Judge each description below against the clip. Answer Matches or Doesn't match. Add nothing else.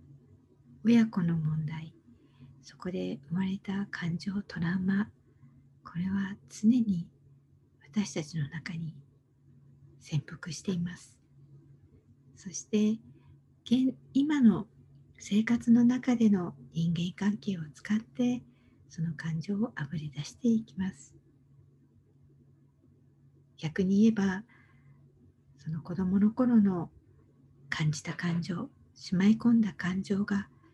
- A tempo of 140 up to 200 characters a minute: Matches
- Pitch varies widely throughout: Matches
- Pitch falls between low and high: Matches